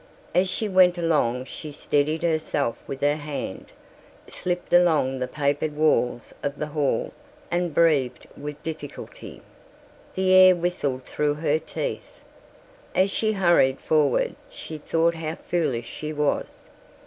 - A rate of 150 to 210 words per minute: No, slow, 135 wpm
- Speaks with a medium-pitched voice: Yes, medium, 155 Hz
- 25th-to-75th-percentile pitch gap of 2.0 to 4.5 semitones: Yes, average, 3.2 semitones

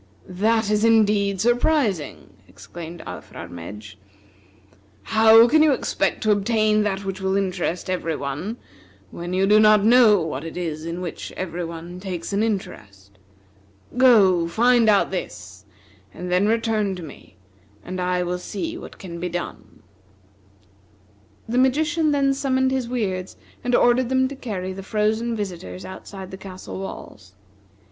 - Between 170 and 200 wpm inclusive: No, average, 145 wpm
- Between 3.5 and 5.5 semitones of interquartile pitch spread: Yes, average, 4.3 semitones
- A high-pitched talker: Yes, high, 200 Hz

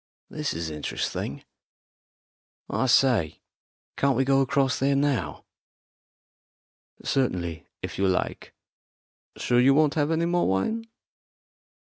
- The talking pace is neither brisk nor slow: No, slow, 110 wpm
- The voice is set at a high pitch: No, low, 135 Hz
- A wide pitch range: Yes, wide, 7.3 semitones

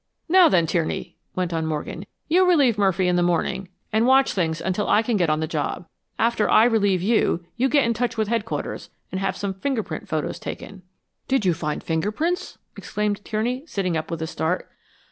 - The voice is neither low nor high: No, high, 200 Hz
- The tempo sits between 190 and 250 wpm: Yes, average, 200 wpm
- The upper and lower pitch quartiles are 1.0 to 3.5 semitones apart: No, average, 5.3 semitones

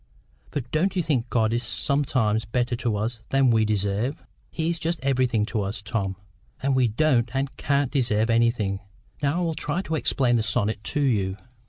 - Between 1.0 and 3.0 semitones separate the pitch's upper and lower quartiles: No, average, 4.4 semitones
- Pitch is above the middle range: No, low, 120 Hz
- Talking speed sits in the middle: Yes, average, 190 wpm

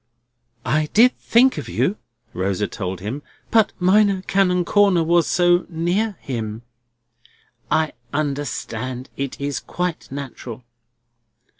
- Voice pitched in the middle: Yes, medium, 160 Hz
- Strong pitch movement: Yes, wide, 6.4 semitones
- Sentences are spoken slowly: Yes, slow, 115 wpm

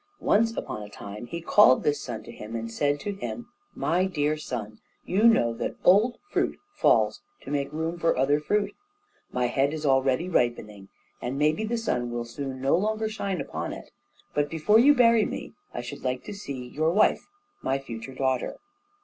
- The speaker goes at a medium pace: Yes, average, 190 wpm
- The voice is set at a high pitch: No, medium, 145 Hz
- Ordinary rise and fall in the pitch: No, wide, 8.0 semitones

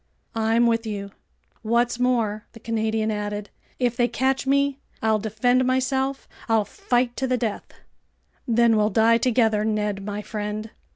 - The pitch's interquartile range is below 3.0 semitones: Yes, narrow, 2.6 semitones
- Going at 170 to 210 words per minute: No, average, 150 wpm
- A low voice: No, high, 225 Hz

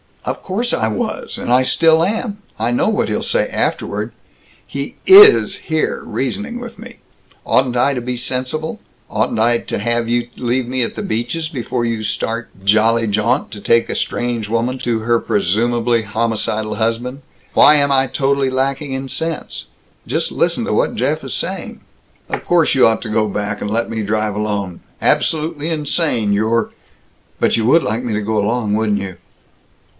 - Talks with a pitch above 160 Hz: No, low, 120 Hz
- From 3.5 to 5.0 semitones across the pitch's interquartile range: Yes, average, 4.0 semitones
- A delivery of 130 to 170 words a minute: No, average, 180 wpm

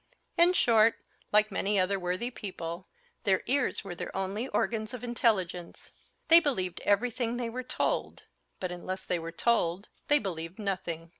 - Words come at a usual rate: Yes, average, 155 wpm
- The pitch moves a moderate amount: Yes, average, 4.7 semitones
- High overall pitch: Yes, high, 200 Hz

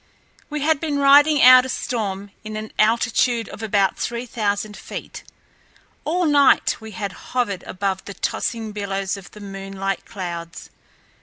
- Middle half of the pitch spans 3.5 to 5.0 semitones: Yes, average, 4.4 semitones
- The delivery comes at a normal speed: Yes, average, 150 wpm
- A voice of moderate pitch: No, high, 215 Hz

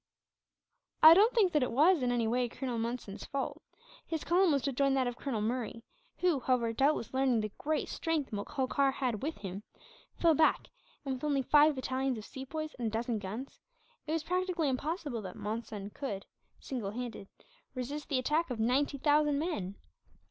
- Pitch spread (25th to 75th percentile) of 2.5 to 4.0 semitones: No, average, 4.5 semitones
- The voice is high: Yes, very high, 265 Hz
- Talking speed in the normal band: Yes, average, 180 wpm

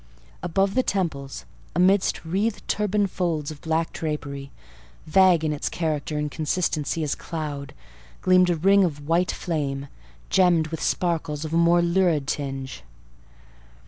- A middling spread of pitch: Yes, average, 3.5 semitones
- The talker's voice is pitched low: No, medium, 160 Hz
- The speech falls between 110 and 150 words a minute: Yes, average, 140 wpm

